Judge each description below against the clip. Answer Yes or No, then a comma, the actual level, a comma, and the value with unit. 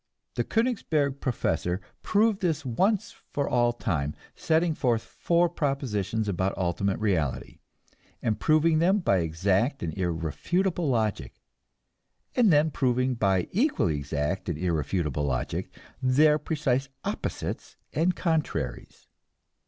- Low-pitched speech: Yes, low, 120 Hz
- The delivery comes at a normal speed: No, slow, 115 wpm